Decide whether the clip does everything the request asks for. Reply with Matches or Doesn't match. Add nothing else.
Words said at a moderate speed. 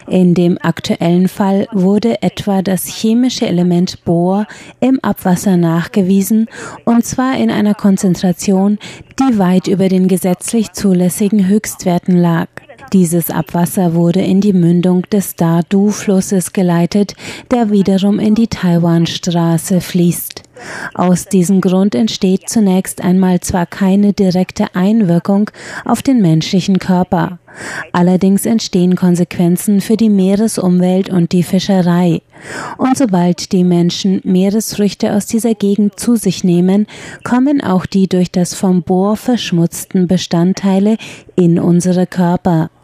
Doesn't match